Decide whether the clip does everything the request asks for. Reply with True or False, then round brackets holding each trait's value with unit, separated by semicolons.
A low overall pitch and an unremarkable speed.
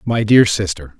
True (105 Hz; 180 wpm)